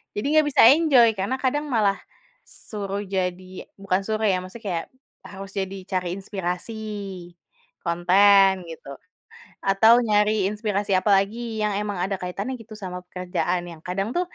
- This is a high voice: Yes, high, 200 Hz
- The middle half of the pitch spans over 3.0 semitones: No, average, 2.7 semitones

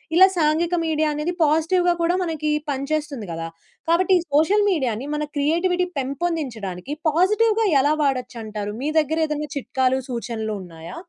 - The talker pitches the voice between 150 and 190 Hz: No, very high, 300 Hz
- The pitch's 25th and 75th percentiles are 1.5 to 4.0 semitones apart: No, average, 5.0 semitones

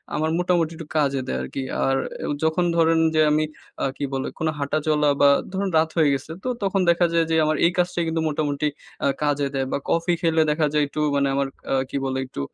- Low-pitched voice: No, medium, 155 Hz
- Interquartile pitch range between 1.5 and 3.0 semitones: Yes, narrow, 2.6 semitones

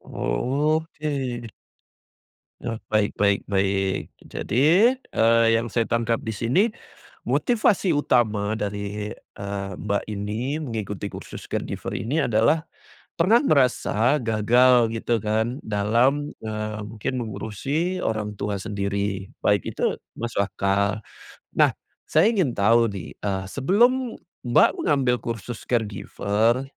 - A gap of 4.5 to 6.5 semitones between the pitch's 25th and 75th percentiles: Yes, average, 4.8 semitones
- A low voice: Yes, low, 115 Hz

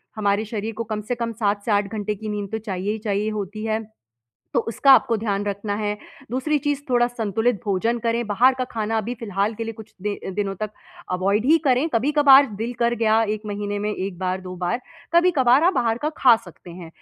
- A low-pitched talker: No, high, 220 Hz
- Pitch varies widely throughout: No, average, 2.9 semitones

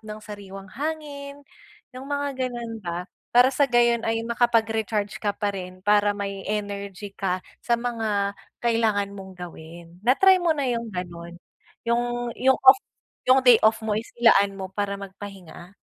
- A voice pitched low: No, high, 215 Hz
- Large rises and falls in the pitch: No, average, 3.5 semitones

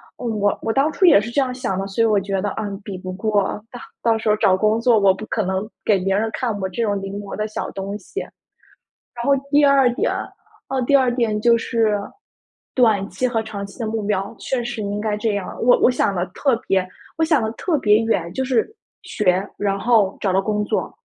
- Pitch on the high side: Yes, high, 215 Hz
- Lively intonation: No, average, 3.3 semitones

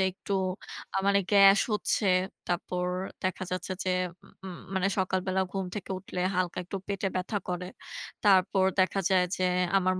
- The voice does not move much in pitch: Yes, narrow, 1.2 semitones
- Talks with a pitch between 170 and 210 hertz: Yes, medium, 185 Hz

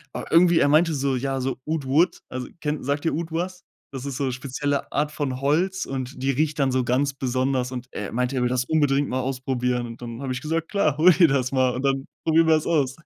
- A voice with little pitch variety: No, average, 3.3 semitones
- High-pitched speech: No, low, 135 Hz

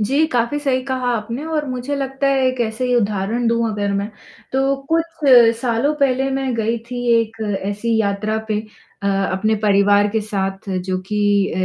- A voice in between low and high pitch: No, high, 230 Hz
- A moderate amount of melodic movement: Yes, average, 4.2 semitones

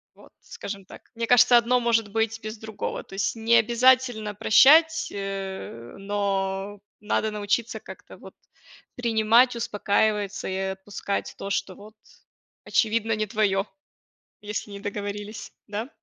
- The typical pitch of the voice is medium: No, high, 215 Hz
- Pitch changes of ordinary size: No, narrow, 2.3 semitones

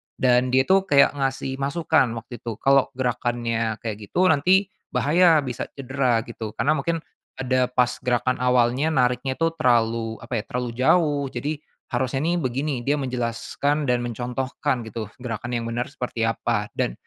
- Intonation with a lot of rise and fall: No, average, 3.0 semitones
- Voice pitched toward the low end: Yes, low, 125 Hz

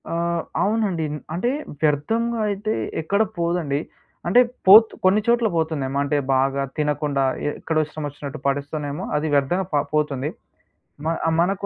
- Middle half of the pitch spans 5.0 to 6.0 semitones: Yes, wide, 5.4 semitones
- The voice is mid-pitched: Yes, medium, 155 Hz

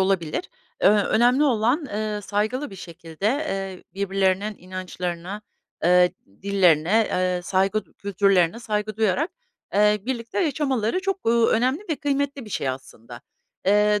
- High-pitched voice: Yes, high, 210 Hz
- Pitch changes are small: No, average, 4.1 semitones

